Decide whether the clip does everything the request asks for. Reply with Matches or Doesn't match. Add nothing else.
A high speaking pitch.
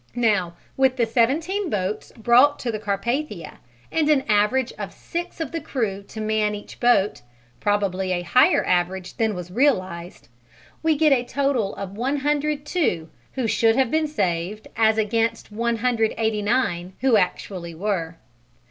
Matches